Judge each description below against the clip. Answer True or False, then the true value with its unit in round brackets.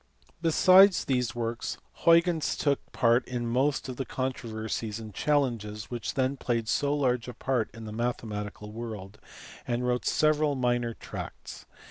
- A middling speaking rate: True (145 wpm)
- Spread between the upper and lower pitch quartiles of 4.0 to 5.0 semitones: False (3.4 semitones)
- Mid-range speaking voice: False (120 Hz)